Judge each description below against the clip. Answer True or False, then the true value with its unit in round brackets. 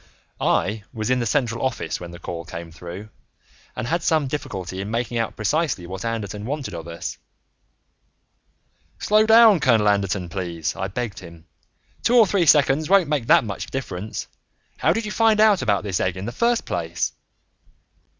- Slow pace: False (175 wpm)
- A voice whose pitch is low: True (110 Hz)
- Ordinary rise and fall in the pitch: False (8.2 semitones)